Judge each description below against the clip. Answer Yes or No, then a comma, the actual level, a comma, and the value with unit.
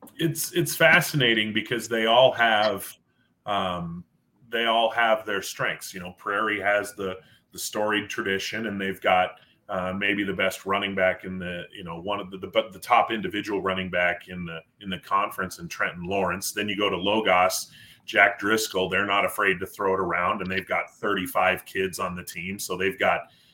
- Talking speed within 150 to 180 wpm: No, average, 195 wpm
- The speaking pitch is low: Yes, low, 100 Hz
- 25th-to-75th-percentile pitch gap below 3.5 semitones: Yes, average, 3.0 semitones